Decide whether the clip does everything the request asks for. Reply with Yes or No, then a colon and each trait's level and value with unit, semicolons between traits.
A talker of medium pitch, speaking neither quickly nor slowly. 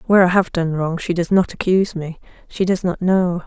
No: medium, 175 Hz; fast, 225 wpm